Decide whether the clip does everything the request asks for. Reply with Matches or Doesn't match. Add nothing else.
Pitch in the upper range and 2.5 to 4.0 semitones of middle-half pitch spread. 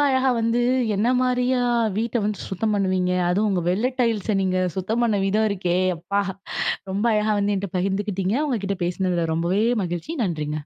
Matches